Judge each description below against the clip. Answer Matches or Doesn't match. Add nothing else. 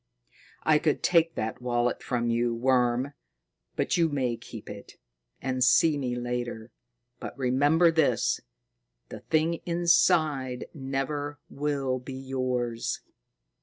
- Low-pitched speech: Matches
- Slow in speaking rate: Matches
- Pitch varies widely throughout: Doesn't match